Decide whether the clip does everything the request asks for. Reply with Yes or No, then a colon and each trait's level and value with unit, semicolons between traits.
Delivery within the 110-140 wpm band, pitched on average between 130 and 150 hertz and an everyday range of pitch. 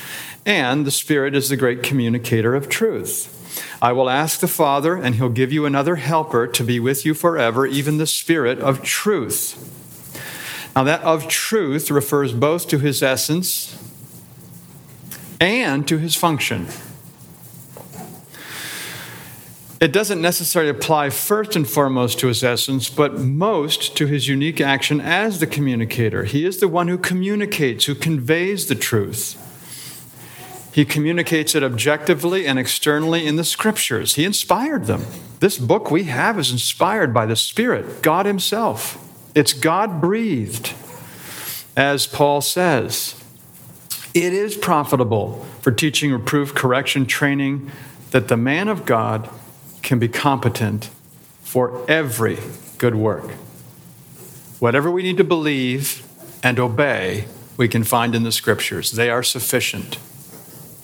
Yes: slow, 135 wpm; medium, 140 Hz; average, 4.5 semitones